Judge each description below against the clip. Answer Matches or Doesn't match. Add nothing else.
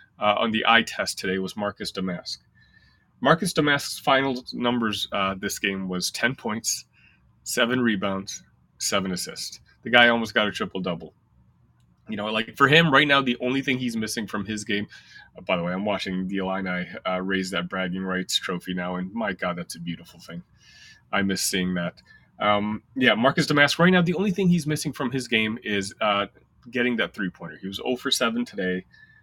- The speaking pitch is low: Matches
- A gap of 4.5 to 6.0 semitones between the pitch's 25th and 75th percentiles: Matches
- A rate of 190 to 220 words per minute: Matches